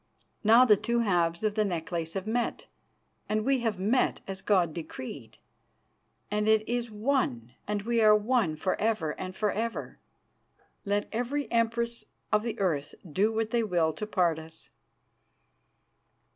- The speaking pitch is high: Yes, high, 210 Hz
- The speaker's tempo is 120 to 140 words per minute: No, average, 155 wpm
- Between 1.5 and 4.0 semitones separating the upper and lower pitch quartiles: No, average, 4.7 semitones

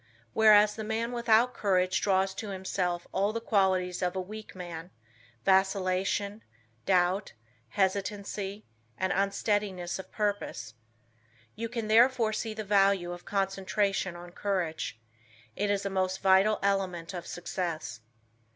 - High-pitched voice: Yes, high, 195 Hz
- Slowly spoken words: Yes, slow, 130 wpm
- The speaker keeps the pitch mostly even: Yes, narrow, 2.2 semitones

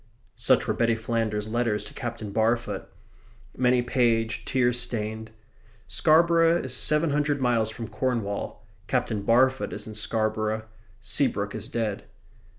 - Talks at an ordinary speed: No, slow, 130 wpm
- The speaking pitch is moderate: No, low, 115 Hz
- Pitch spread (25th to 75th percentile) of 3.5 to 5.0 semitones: No, average, 2.7 semitones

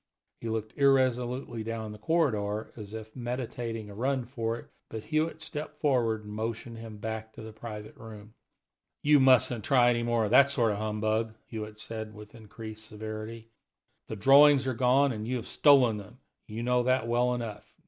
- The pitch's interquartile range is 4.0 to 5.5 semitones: No, average, 2.7 semitones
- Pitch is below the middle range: Yes, low, 115 Hz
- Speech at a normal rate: Yes, average, 185 wpm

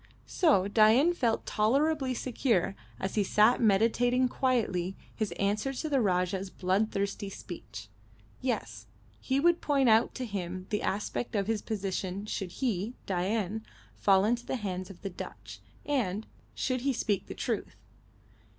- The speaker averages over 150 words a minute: No, average, 145 wpm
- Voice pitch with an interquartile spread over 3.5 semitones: Yes, average, 4.7 semitones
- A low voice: No, high, 215 Hz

